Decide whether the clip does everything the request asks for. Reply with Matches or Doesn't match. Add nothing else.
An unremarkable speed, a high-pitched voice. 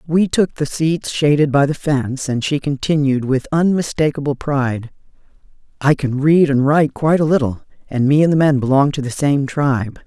Doesn't match